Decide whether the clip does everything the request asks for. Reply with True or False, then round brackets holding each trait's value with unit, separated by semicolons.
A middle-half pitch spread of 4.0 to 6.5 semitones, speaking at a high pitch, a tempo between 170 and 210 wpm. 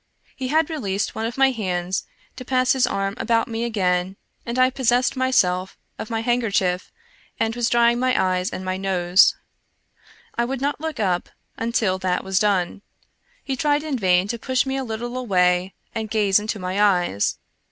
True (5.2 semitones; 220 Hz; 180 wpm)